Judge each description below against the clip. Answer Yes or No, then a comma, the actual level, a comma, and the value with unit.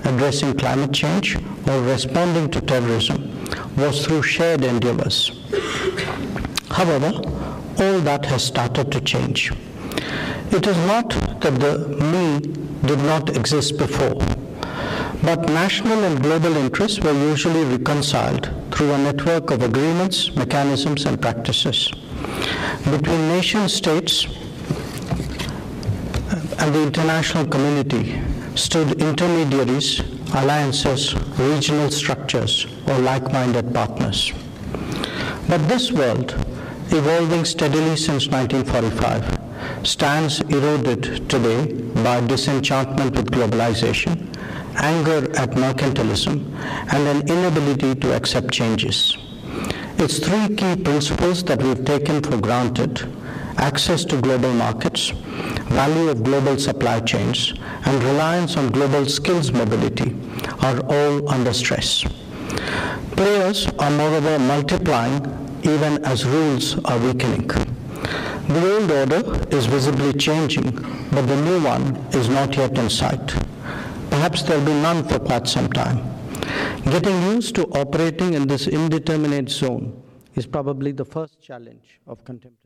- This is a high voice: No, medium, 140 Hz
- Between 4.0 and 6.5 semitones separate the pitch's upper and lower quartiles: No, average, 3.3 semitones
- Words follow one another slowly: Yes, slow, 115 wpm